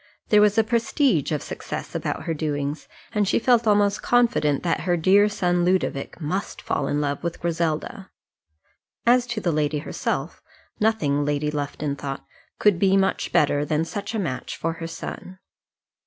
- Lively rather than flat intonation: Yes, wide, 5.8 semitones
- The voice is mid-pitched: Yes, medium, 175 Hz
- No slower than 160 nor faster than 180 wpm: Yes, average, 170 wpm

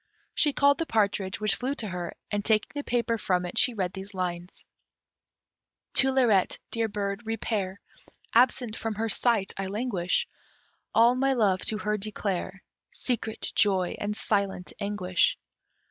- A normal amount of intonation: Yes, average, 3.4 semitones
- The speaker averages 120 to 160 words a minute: Yes, average, 150 wpm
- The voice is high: Yes, high, 210 Hz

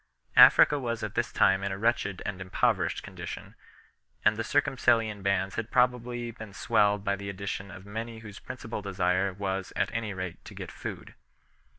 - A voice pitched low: Yes, low, 105 Hz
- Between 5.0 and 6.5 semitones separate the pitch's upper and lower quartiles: No, average, 3.1 semitones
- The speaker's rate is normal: Yes, average, 175 wpm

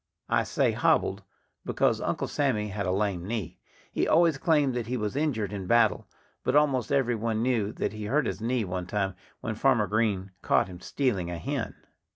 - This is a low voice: Yes, low, 110 Hz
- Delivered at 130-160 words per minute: No, average, 195 wpm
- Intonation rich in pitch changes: No, average, 4.4 semitones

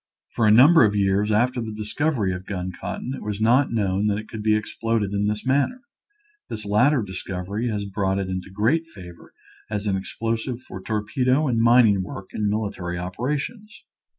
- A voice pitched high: No, low, 105 Hz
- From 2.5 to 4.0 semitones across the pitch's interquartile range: Yes, average, 3.7 semitones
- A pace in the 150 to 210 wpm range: Yes, average, 180 wpm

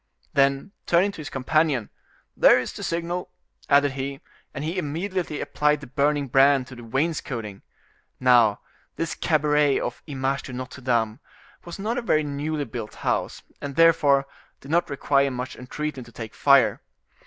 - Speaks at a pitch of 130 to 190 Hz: Yes, medium, 140 Hz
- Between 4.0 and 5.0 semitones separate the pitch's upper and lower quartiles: No, average, 3.2 semitones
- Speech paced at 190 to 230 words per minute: No, average, 165 wpm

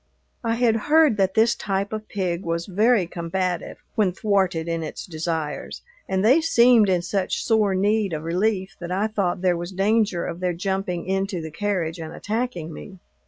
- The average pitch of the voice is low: No, high, 190 Hz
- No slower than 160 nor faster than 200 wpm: Yes, average, 180 wpm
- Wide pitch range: No, average, 3.7 semitones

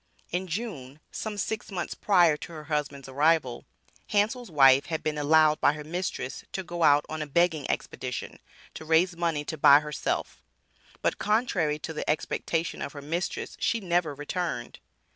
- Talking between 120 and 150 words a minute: No, average, 165 wpm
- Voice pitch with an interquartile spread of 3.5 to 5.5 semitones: No, average, 3.1 semitones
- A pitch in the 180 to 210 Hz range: No, medium, 160 Hz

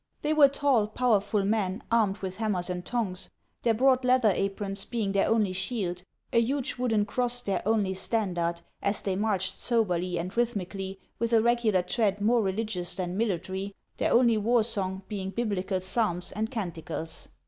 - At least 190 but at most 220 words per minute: No, average, 165 wpm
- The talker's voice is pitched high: Yes, high, 205 Hz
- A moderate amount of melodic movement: Yes, average, 3.6 semitones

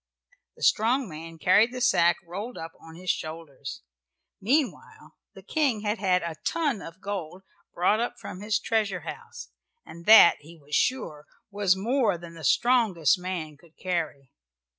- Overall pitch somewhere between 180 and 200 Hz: Yes, medium, 185 Hz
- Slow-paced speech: No, average, 160 wpm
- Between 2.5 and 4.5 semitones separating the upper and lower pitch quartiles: No, average, 4.9 semitones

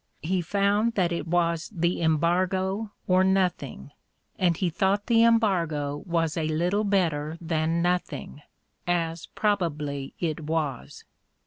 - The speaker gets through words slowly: Yes, slow, 125 wpm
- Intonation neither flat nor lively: Yes, average, 3.1 semitones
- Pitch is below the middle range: No, medium, 170 Hz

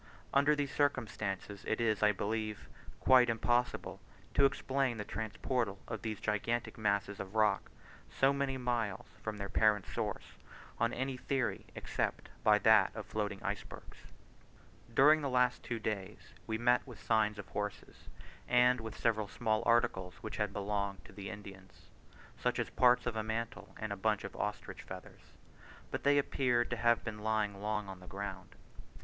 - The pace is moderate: Yes, average, 165 wpm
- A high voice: No, low, 110 Hz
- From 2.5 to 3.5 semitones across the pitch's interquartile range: Yes, average, 3.0 semitones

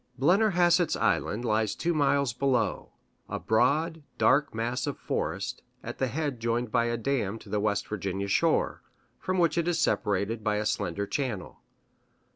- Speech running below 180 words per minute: Yes, average, 160 wpm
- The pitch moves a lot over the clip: Yes, wide, 5.8 semitones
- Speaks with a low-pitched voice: Yes, low, 120 Hz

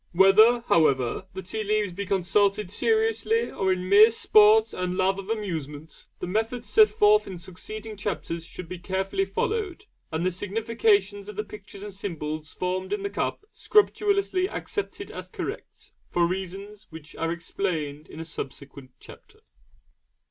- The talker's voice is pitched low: No, high, 195 Hz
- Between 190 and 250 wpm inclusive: No, average, 155 wpm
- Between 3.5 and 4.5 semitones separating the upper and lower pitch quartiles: Yes, average, 3.9 semitones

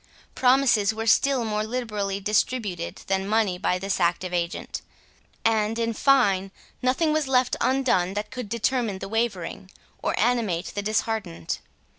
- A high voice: Yes, high, 215 Hz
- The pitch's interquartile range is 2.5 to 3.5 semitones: No, average, 4.2 semitones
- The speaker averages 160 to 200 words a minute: No, average, 140 wpm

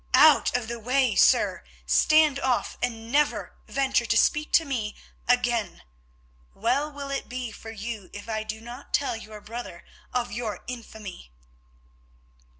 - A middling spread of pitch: Yes, average, 3.5 semitones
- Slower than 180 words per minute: Yes, average, 150 wpm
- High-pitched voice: Yes, high, 240 Hz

